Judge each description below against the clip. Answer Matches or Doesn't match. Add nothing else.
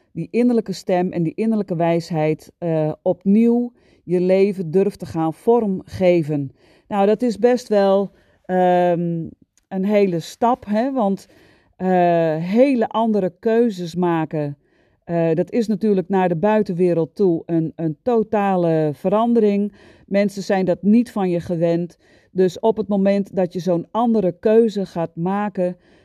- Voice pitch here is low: Doesn't match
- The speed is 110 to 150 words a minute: Matches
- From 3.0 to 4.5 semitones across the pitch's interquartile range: Matches